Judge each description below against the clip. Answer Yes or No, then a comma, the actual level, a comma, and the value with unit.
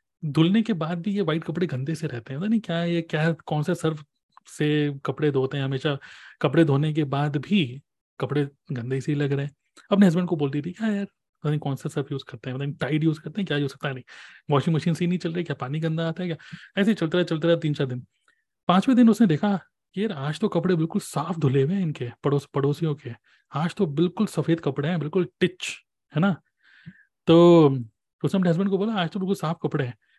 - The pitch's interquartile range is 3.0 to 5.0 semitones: Yes, average, 3.8 semitones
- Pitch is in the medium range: Yes, medium, 160 Hz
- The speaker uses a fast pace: Yes, fast, 245 wpm